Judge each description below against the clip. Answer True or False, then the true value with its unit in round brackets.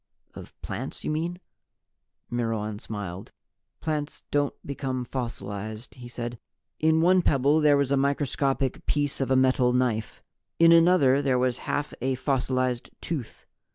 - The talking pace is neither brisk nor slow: True (145 wpm)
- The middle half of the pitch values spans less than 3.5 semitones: True (3.1 semitones)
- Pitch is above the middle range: False (130 Hz)